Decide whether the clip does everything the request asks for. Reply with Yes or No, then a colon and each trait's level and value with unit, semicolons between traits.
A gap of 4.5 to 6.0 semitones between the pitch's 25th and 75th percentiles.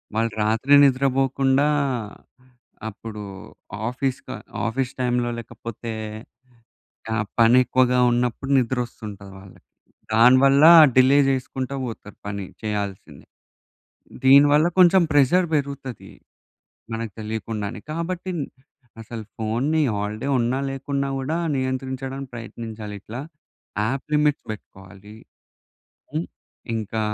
No: average, 3.5 semitones